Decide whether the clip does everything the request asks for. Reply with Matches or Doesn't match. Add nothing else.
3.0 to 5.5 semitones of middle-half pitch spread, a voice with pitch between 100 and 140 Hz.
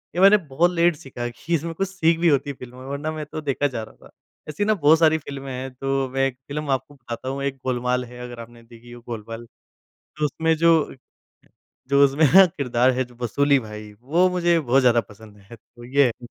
Matches